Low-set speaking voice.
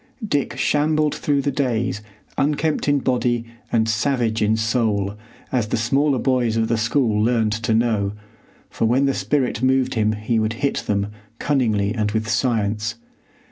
Yes: low, 115 Hz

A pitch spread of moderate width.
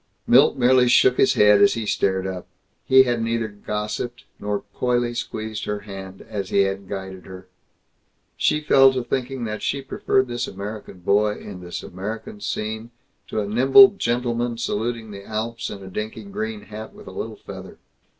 Yes: average, 3.2 semitones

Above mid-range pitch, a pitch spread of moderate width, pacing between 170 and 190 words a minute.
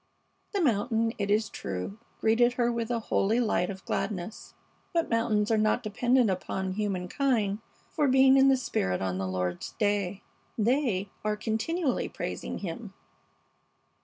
No: high, 215 Hz; average, 3.8 semitones; average, 145 wpm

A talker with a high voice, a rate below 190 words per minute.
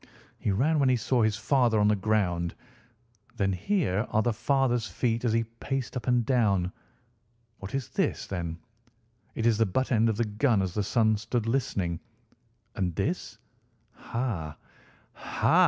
No: low, 110 Hz; average, 165 wpm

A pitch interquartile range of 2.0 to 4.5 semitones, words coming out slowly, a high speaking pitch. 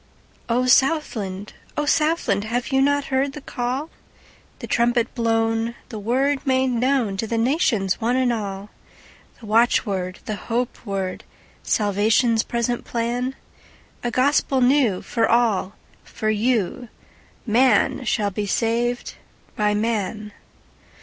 Yes: average, 3.3 semitones; slow, 105 wpm; high, 235 Hz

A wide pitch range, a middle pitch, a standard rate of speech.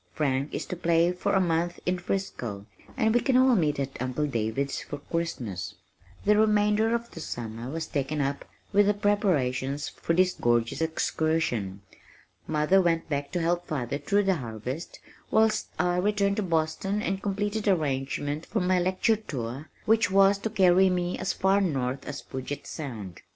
Yes: wide, 6.1 semitones; medium, 165 Hz; average, 170 wpm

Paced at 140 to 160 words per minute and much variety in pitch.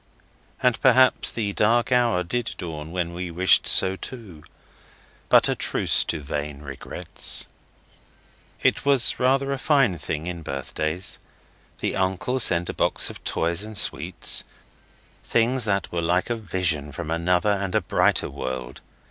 Yes: average, 150 wpm; wide, 6.0 semitones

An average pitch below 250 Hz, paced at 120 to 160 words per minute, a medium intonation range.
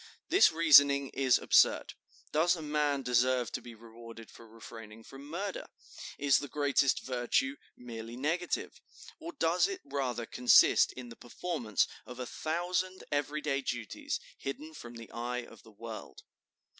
Yes: low, 135 Hz; average, 150 wpm; average, 4.4 semitones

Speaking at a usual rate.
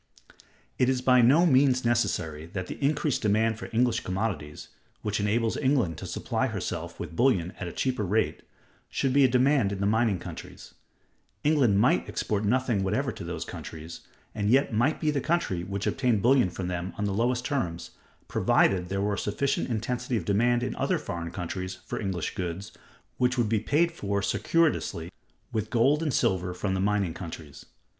Yes: average, 180 wpm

